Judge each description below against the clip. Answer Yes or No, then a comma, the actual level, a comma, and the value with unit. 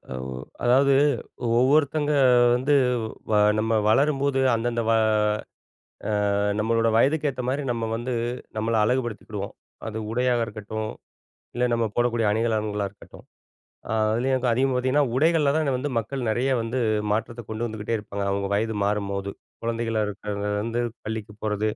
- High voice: No, low, 115 Hz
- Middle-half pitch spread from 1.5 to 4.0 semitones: Yes, average, 3.2 semitones